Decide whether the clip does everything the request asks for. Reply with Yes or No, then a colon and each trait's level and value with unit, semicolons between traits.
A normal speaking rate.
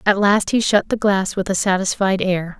No: fast, 230 wpm